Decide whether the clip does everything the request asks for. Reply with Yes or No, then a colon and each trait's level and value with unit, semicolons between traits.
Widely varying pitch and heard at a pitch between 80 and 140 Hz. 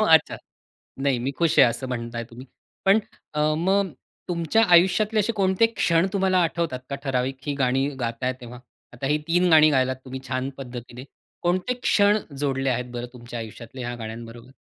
Yes: wide, 6.2 semitones; low, 135 Hz